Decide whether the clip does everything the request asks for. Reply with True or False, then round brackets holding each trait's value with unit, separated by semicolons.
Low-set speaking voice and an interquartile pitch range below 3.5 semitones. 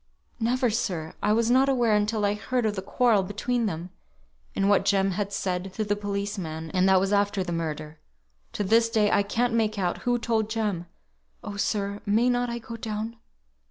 False (205 Hz; 2.9 semitones)